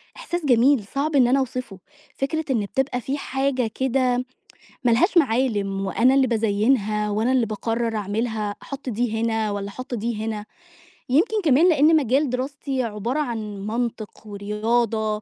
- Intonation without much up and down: No, average, 3.8 semitones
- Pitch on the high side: Yes, high, 240 Hz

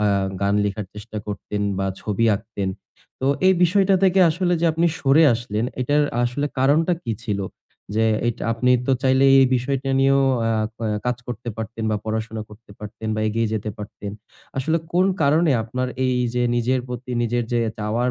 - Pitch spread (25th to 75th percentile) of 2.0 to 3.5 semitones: No, average, 4.0 semitones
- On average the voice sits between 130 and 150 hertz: No, low, 120 Hz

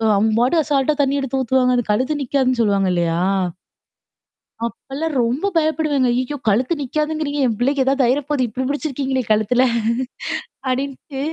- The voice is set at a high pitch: Yes, very high, 265 Hz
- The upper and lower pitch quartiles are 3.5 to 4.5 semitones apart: No, average, 3.0 semitones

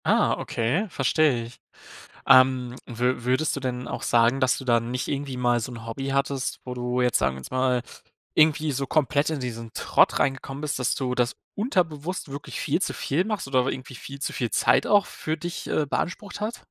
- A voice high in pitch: No, low, 130 Hz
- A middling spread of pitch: Yes, average, 3.3 semitones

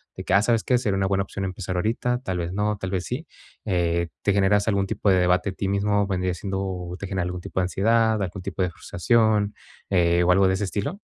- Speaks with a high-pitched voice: No, very low, 95 Hz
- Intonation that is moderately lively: No, narrow, 2.3 semitones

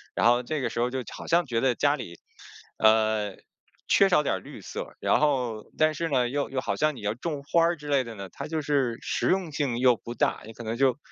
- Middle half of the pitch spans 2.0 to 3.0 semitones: No, average, 4.4 semitones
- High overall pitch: No, low, 130 Hz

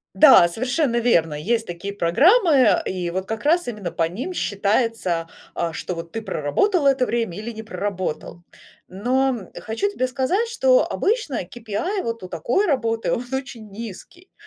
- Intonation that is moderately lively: No, wide, 6.5 semitones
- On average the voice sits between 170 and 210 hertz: No, high, 230 Hz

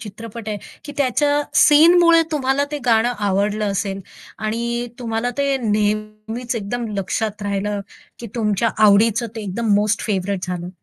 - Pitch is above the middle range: Yes, high, 220 Hz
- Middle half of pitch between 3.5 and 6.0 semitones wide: No, average, 2.9 semitones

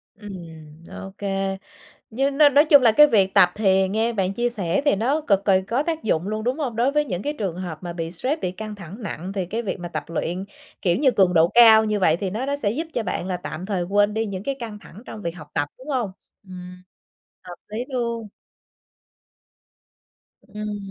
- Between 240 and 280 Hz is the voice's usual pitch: No, high, 205 Hz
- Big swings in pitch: No, average, 4.7 semitones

